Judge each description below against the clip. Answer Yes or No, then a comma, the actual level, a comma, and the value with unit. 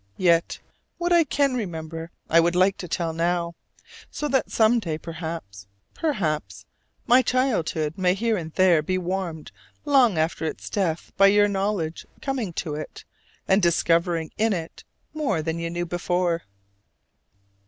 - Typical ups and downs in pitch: Yes, average, 4.3 semitones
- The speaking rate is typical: Yes, average, 150 wpm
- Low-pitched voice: No, medium, 175 Hz